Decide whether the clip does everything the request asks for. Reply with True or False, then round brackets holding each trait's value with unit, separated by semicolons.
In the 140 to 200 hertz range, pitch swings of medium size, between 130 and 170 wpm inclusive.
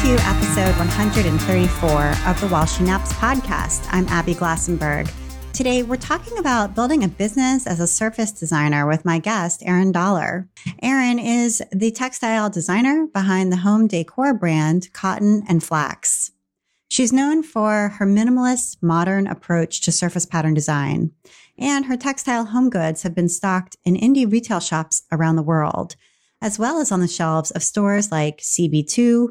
False (185 Hz; 6.3 semitones; 160 wpm)